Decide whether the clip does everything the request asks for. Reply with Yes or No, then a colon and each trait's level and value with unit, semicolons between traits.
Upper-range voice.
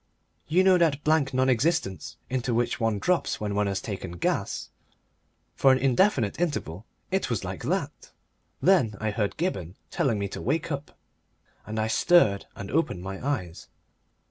No: low, 120 Hz